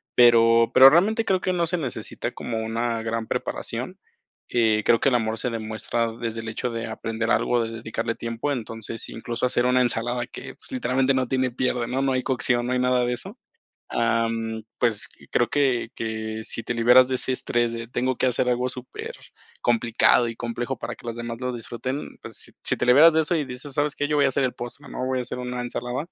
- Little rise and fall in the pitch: Yes, narrow, 2.0 semitones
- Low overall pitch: Yes, low, 120 Hz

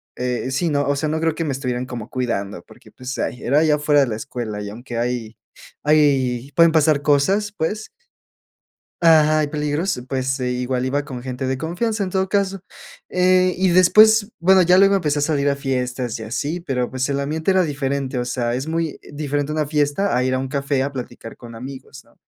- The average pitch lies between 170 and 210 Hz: No, medium, 140 Hz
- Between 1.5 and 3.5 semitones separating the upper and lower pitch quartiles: No, average, 4.2 semitones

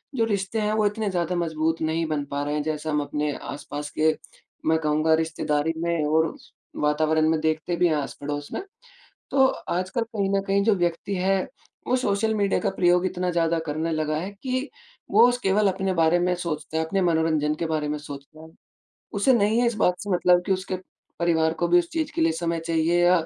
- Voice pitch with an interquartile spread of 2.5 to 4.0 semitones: Yes, average, 3.7 semitones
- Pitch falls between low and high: Yes, medium, 170 Hz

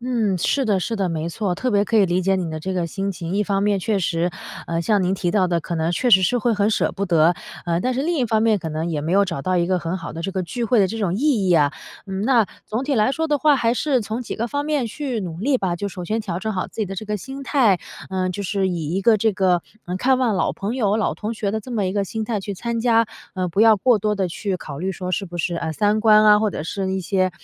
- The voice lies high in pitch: Yes, high, 200 Hz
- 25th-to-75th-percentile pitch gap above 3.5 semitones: Yes, average, 3.9 semitones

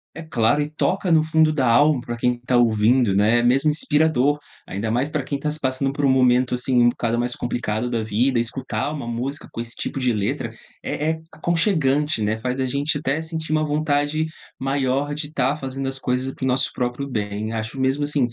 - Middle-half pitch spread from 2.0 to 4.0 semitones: Yes, average, 3.5 semitones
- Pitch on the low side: Yes, low, 130 Hz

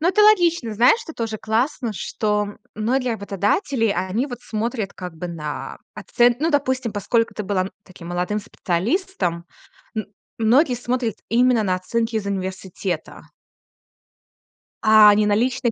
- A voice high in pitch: Yes, high, 220 Hz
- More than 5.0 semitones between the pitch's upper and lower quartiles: No, average, 4.2 semitones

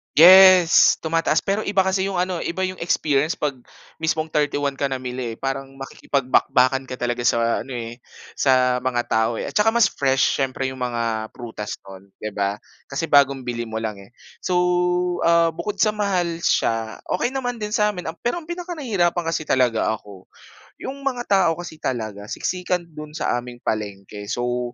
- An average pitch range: No, wide, 6.7 semitones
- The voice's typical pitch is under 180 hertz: Yes, medium, 140 Hz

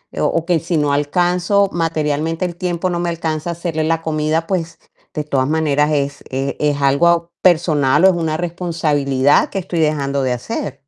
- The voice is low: No, medium, 160 Hz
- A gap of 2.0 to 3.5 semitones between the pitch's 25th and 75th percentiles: Yes, average, 2.8 semitones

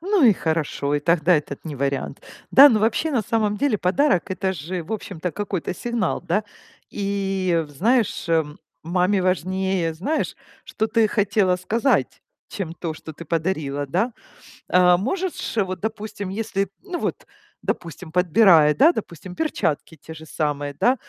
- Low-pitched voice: No, medium, 185 Hz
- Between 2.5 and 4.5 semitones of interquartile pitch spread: No, average, 5.0 semitones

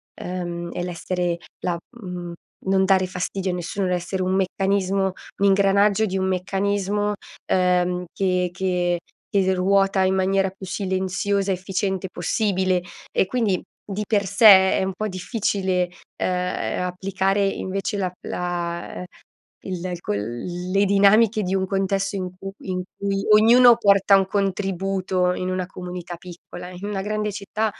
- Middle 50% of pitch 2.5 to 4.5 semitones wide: No, narrow, 1.6 semitones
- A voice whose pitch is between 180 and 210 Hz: Yes, high, 190 Hz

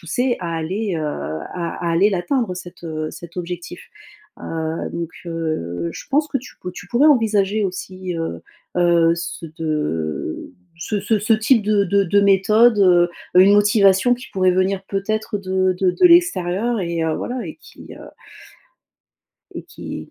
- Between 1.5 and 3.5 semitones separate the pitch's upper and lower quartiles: No, average, 3.9 semitones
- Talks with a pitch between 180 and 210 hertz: Yes, medium, 185 Hz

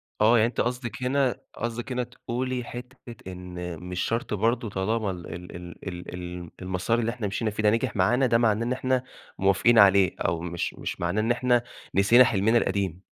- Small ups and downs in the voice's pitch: No, average, 4.6 semitones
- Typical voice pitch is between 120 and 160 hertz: No, low, 110 Hz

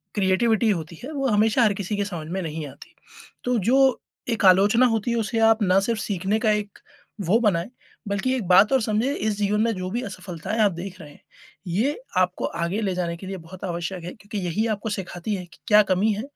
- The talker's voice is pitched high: Yes, high, 205 Hz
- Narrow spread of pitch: No, average, 3.3 semitones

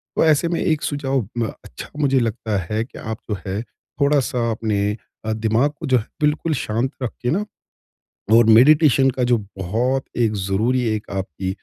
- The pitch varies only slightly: No, average, 4.2 semitones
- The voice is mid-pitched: No, low, 120 Hz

